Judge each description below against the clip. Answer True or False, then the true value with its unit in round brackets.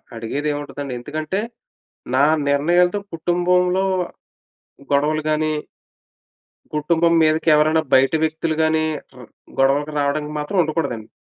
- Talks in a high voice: False (155 Hz)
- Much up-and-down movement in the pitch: False (2.5 semitones)